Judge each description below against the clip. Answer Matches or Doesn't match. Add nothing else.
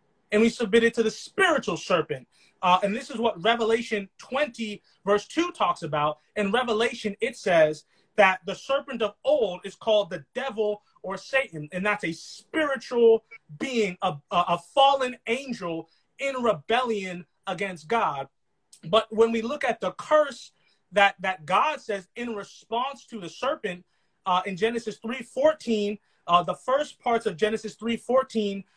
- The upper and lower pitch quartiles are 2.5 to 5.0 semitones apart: Matches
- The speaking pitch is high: Matches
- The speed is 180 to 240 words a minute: Doesn't match